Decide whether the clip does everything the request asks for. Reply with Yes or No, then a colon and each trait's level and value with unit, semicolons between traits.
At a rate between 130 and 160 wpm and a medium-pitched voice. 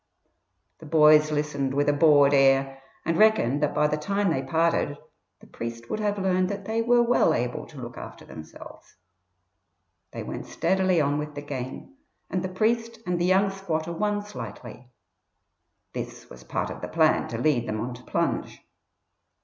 No: average, 175 wpm; medium, 150 Hz